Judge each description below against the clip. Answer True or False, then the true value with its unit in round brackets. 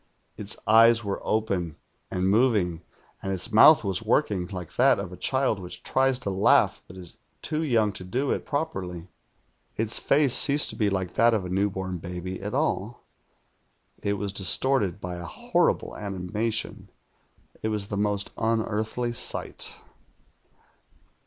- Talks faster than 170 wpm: False (155 wpm)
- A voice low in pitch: True (105 Hz)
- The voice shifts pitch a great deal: False (3.7 semitones)